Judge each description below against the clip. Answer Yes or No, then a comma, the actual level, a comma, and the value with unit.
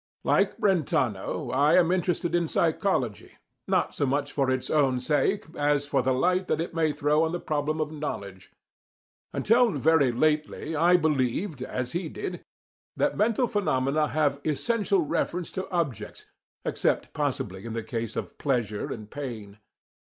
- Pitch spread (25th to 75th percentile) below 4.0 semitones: No, average, 4.8 semitones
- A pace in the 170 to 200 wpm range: No, average, 155 wpm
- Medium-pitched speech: Yes, medium, 150 Hz